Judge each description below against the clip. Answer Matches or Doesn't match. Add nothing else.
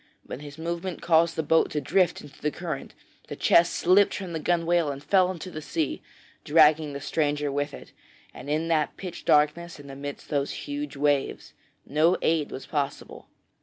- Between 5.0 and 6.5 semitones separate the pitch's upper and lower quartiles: Doesn't match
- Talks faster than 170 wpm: Matches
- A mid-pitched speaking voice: Matches